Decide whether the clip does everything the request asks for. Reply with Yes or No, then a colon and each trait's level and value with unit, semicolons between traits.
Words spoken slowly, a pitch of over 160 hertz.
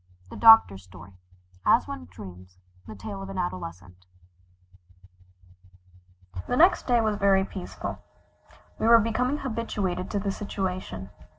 Yes: slow, 130 wpm; medium, 185 Hz